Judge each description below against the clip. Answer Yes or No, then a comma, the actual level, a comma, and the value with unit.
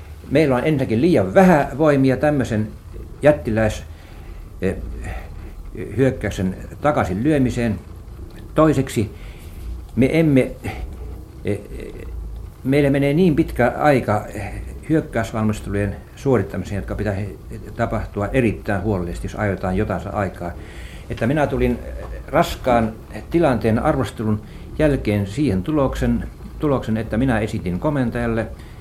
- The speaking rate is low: Yes, slow, 90 wpm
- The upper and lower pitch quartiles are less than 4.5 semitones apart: No, wide, 5.6 semitones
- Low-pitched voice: Yes, low, 110 Hz